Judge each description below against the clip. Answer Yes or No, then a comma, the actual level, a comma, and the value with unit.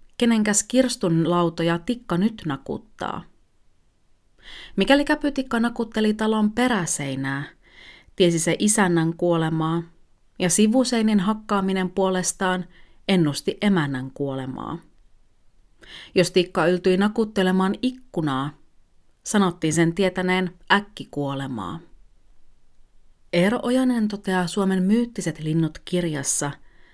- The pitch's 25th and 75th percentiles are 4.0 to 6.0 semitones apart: Yes, average, 4.5 semitones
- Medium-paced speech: No, slow, 85 wpm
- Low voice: No, medium, 185 Hz